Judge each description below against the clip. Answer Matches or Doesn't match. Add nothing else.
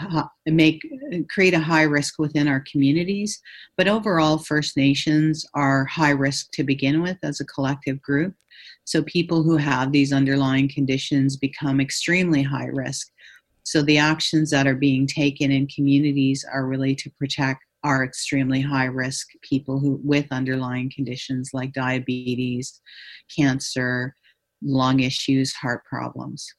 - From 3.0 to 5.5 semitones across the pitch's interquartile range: Doesn't match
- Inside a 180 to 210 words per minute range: Doesn't match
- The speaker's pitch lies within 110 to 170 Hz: Matches